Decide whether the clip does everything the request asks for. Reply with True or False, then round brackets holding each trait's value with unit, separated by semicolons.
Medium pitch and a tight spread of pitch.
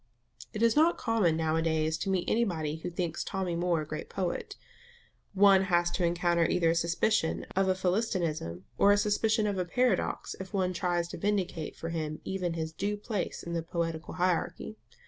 False (175 Hz; 3.3 semitones)